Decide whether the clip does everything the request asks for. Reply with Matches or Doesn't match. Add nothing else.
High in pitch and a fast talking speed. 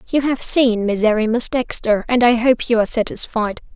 Doesn't match